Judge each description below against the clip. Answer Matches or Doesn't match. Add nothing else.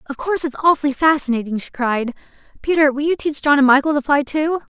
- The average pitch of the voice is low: Doesn't match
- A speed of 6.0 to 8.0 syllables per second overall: Matches